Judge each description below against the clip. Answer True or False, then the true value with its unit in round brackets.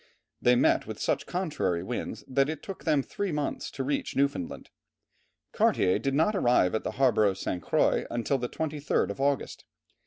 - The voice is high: False (135 Hz)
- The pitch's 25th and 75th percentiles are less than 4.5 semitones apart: True (3.9 semitones)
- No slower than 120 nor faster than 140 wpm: False (180 wpm)